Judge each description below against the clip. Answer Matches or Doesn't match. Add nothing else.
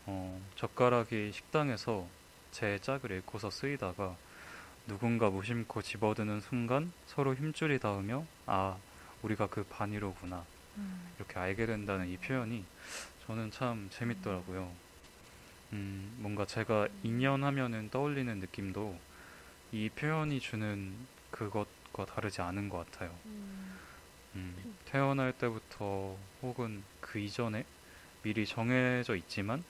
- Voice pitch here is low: Matches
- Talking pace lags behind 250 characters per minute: Doesn't match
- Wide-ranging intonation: Doesn't match